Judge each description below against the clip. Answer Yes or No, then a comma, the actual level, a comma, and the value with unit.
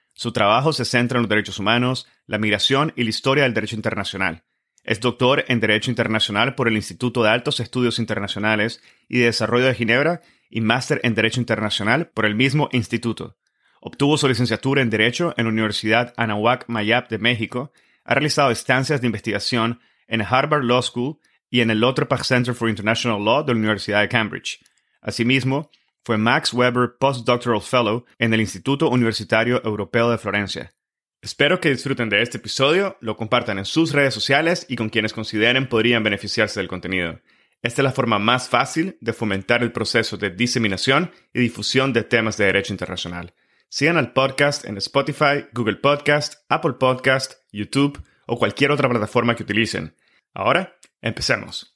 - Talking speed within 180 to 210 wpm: No, average, 170 wpm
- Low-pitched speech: Yes, low, 120 Hz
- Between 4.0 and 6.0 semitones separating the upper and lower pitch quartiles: No, average, 3.3 semitones